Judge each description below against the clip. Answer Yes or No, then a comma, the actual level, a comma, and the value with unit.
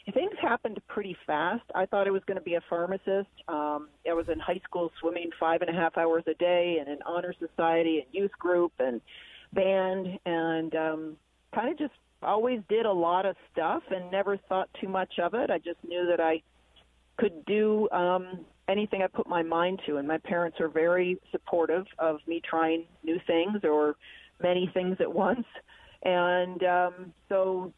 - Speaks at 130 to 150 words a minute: No, average, 190 wpm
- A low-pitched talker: No, medium, 175 Hz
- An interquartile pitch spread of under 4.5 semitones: Yes, narrow, 2.6 semitones